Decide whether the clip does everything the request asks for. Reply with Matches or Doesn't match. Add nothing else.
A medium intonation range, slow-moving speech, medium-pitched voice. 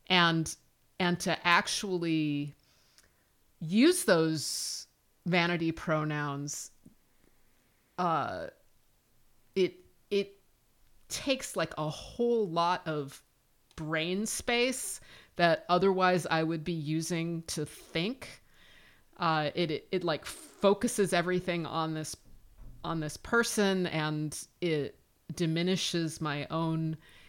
Matches